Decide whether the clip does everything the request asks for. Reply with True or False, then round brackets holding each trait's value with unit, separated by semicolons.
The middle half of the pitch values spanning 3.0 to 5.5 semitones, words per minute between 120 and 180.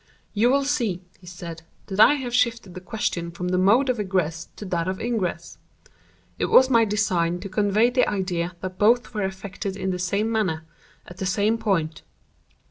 False (3.8 semitones; 190 wpm)